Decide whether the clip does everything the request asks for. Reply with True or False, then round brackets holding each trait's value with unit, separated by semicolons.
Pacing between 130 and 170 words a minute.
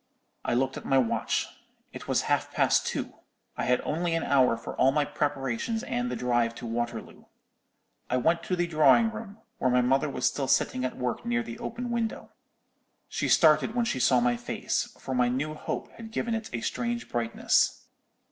False (195 wpm)